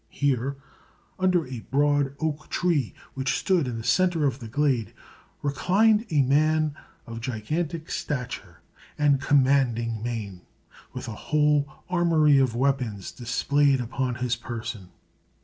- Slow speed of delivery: Yes, slow, 130 wpm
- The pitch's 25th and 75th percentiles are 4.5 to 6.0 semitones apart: No, average, 4.1 semitones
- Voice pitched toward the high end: No, medium, 140 Hz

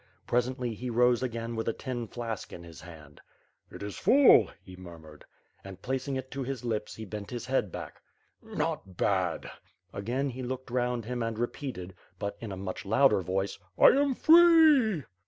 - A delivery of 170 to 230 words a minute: Yes, average, 175 wpm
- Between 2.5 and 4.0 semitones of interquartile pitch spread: No, average, 5.1 semitones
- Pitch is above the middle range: No, low, 120 Hz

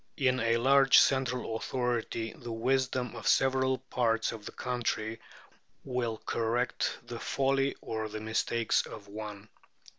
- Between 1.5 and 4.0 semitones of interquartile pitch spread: Yes, average, 2.7 semitones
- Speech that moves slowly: Yes, slow, 130 wpm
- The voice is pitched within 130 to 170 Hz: No, low, 120 Hz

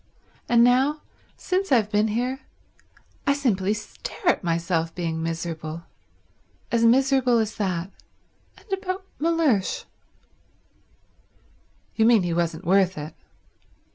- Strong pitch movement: Yes, wide, 7.6 semitones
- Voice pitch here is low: No, high, 215 Hz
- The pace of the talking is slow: Yes, slow, 110 wpm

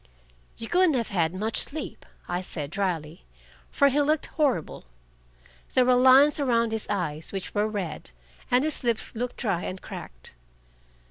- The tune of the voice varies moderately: No, wide, 6.4 semitones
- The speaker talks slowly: No, average, 155 wpm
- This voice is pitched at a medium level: No, high, 220 Hz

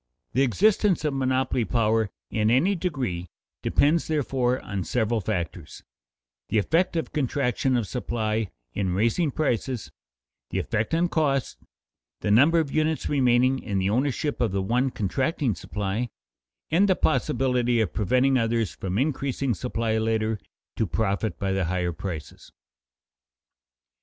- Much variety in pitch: No, average, 4.5 semitones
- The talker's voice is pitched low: Yes, low, 120 Hz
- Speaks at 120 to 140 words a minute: Yes, slow, 135 wpm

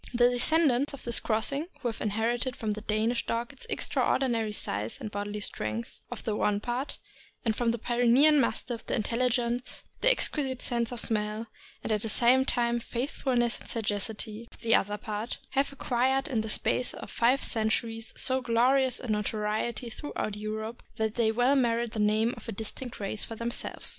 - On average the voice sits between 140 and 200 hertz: No, high, 235 Hz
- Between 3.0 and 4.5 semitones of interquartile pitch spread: No, narrow, 2.4 semitones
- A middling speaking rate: Yes, average, 185 wpm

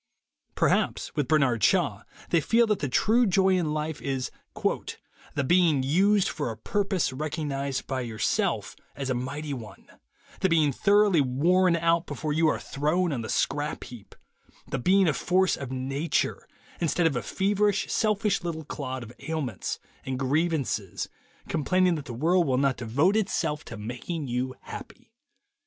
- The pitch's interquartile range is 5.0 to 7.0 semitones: Yes, wide, 5.5 semitones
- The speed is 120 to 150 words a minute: No, average, 165 wpm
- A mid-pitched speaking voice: Yes, medium, 150 Hz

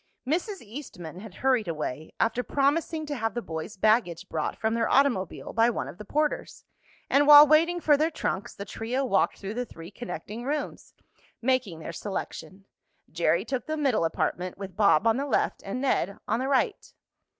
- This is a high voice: Yes, high, 230 Hz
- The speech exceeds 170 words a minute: Yes, average, 185 wpm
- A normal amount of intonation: No, wide, 6.6 semitones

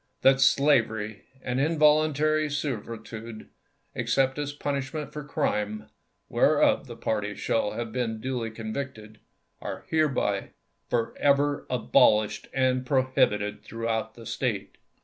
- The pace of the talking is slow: Yes, slow, 110 wpm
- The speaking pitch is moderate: No, low, 125 Hz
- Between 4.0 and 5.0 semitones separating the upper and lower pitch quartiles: Yes, average, 4.4 semitones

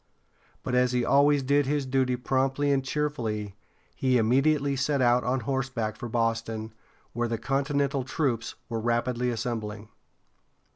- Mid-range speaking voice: No, low, 125 Hz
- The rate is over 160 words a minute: No, average, 140 wpm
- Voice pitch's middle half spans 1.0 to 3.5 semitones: Yes, average, 2.9 semitones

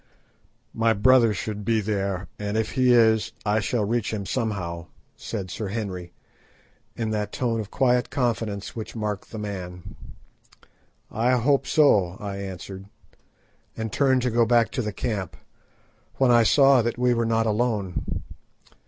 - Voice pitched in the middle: No, low, 110 Hz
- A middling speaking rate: Yes, average, 155 wpm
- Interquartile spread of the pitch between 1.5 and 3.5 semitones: Yes, average, 3.0 semitones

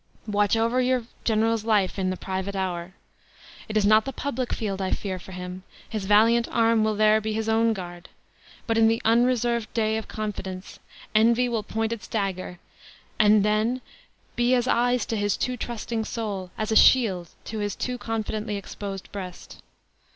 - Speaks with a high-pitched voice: Yes, high, 215 Hz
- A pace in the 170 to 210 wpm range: Yes, average, 175 wpm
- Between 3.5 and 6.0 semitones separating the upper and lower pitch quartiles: No, narrow, 2.5 semitones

